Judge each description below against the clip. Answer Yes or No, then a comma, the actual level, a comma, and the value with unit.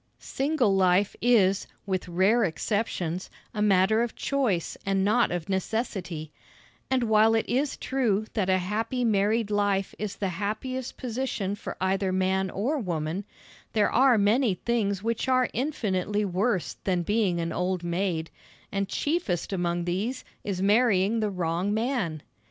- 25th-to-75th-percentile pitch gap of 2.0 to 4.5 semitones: Yes, average, 3.8 semitones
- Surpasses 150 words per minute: No, average, 145 wpm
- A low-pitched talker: No, high, 200 Hz